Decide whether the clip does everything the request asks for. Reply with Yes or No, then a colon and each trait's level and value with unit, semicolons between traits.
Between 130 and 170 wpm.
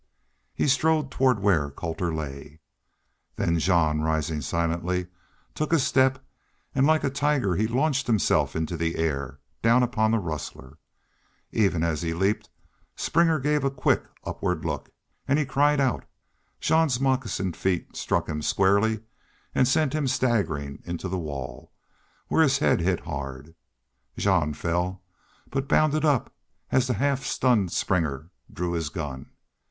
Yes: average, 145 wpm